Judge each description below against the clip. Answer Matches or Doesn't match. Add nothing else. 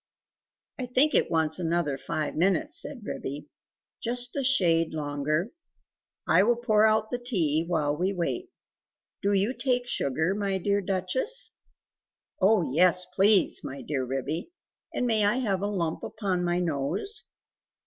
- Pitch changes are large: Matches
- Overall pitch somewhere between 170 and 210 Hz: Matches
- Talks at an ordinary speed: Matches